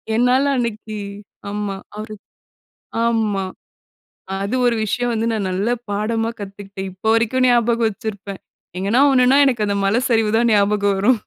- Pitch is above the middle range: Yes, high, 220 Hz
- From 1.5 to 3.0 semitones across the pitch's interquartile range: Yes, average, 2.7 semitones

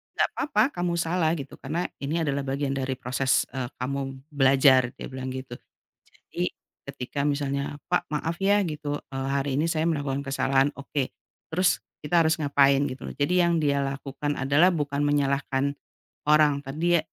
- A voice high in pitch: No, medium, 140 Hz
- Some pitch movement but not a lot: No, narrow, 2.0 semitones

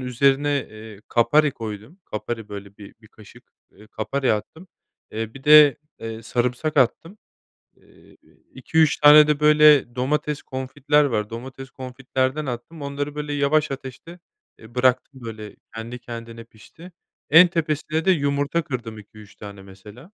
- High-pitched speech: No, low, 130 Hz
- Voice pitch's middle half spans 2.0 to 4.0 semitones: No, average, 4.9 semitones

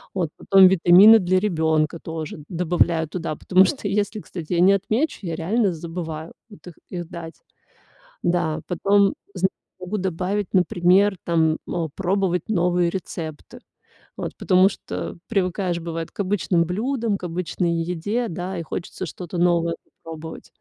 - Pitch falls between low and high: Yes, medium, 180 Hz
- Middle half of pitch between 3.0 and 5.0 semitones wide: No, narrow, 2.6 semitones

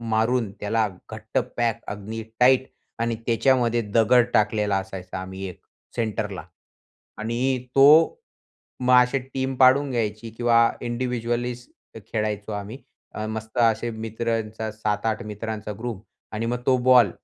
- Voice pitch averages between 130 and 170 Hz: No, low, 115 Hz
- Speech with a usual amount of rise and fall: No, narrow, 2.3 semitones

